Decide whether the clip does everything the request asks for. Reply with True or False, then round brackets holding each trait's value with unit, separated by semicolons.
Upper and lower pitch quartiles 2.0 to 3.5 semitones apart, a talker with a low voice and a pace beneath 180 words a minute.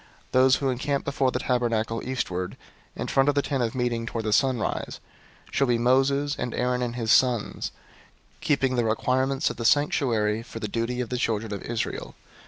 False (2.6 semitones; 125 Hz; 190 wpm)